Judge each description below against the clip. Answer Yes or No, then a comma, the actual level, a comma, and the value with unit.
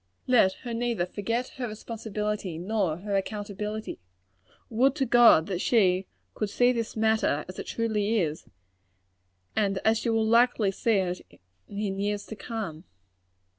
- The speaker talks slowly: No, average, 155 wpm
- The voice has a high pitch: Yes, high, 215 Hz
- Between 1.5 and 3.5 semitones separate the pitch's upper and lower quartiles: Yes, average, 2.9 semitones